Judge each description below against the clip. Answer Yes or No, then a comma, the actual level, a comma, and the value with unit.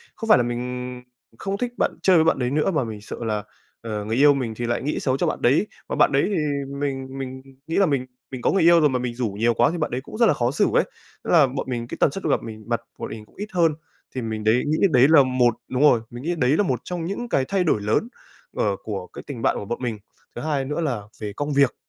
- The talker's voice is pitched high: No, low, 130 Hz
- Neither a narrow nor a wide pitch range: Yes, average, 4.6 semitones